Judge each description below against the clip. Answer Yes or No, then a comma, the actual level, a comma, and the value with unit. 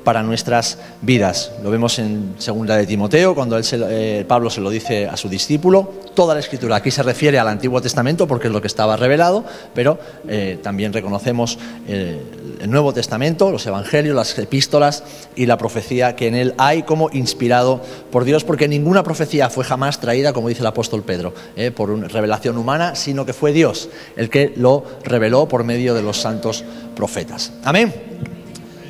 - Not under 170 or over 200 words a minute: Yes, average, 185 wpm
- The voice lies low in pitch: Yes, low, 120 Hz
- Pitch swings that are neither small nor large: Yes, average, 4.4 semitones